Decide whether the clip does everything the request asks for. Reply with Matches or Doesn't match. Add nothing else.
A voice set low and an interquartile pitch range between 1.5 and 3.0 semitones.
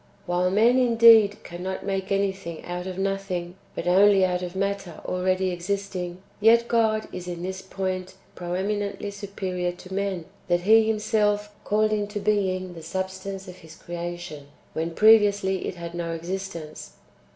Doesn't match